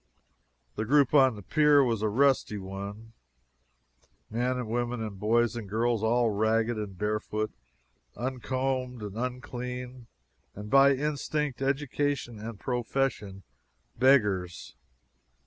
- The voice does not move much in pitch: No, average, 3.5 semitones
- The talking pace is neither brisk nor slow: No, slow, 115 wpm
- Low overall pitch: Yes, low, 120 Hz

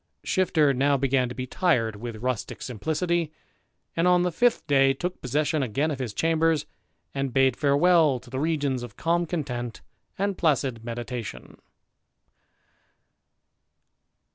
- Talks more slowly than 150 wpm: Yes, slow, 135 wpm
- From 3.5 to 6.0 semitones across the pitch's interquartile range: Yes, average, 4.7 semitones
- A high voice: No, medium, 140 Hz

